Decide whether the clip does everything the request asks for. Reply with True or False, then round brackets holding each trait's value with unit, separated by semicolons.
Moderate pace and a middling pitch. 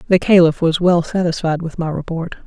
True (195 wpm; 170 Hz)